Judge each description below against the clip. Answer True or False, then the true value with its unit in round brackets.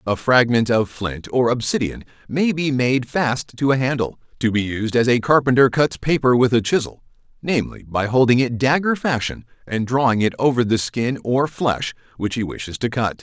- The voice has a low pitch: True (125 Hz)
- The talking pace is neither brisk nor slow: True (195 wpm)